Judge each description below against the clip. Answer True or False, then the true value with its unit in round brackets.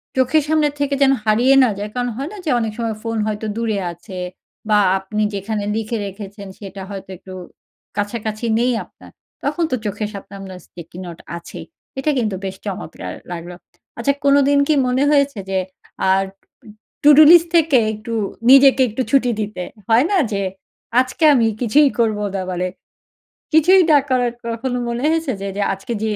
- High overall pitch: True (230 Hz)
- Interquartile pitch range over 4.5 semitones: True (5.2 semitones)